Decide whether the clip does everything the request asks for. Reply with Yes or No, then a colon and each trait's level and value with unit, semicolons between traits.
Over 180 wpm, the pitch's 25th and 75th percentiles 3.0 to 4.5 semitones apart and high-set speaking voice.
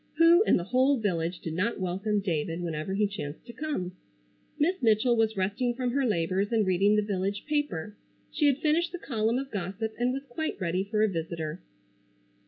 No: average, 190 wpm; wide, 5.6 semitones; high, 210 Hz